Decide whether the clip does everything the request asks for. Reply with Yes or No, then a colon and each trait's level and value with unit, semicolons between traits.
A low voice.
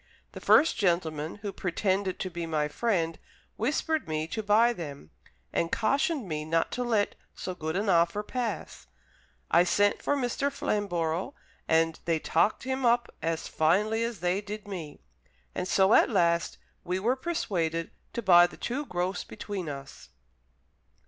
No: medium, 185 Hz